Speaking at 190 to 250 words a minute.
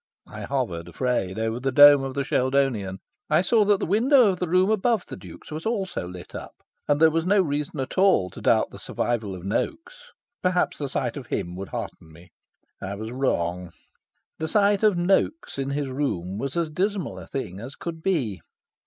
Yes: average, 200 wpm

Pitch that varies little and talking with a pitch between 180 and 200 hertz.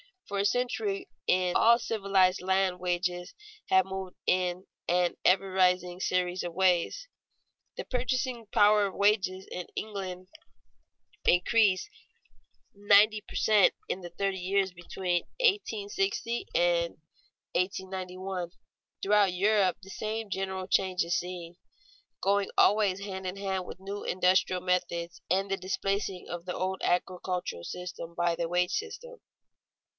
Yes: narrow, 2.1 semitones; high, 190 Hz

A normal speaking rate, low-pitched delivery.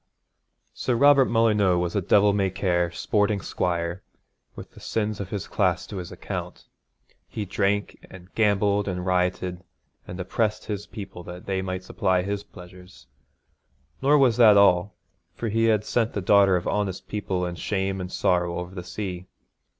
Yes: average, 165 wpm; very low, 95 Hz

